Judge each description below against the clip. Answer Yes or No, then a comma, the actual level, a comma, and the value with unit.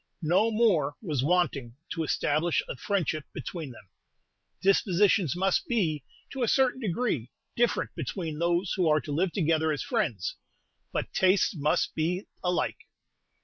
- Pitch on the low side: No, medium, 175 Hz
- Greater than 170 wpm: No, average, 145 wpm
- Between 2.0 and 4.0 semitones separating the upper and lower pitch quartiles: No, average, 4.6 semitones